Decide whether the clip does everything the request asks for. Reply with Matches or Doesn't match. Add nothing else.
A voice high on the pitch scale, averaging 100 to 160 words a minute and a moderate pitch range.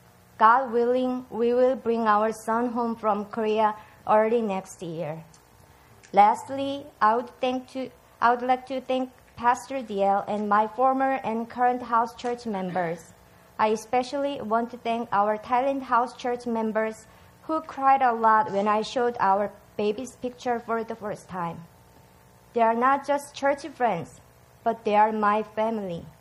Matches